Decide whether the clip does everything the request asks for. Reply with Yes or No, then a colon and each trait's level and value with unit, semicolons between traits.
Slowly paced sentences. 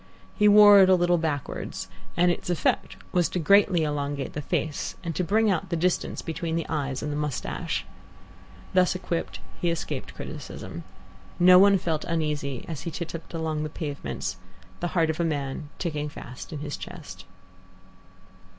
No: average, 170 wpm